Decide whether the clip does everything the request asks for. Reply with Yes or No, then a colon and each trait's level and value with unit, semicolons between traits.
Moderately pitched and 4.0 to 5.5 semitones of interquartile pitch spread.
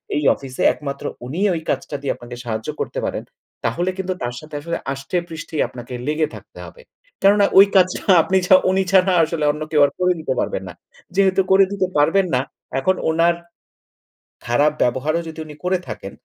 Yes: medium, 160 Hz; average, 5.2 semitones